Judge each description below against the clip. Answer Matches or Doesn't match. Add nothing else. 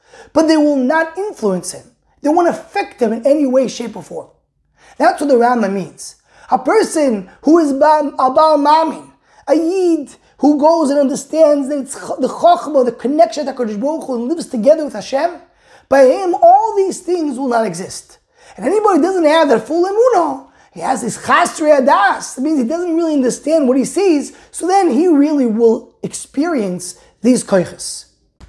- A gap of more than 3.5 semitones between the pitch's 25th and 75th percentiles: Matches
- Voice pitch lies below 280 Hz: Doesn't match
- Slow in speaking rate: Doesn't match